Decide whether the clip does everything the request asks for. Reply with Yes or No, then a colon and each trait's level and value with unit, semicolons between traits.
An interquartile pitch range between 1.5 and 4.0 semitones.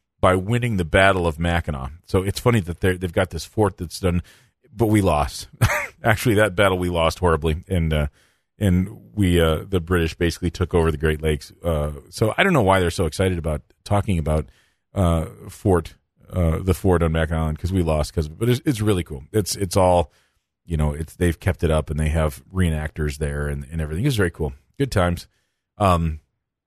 Yes: average, 3.3 semitones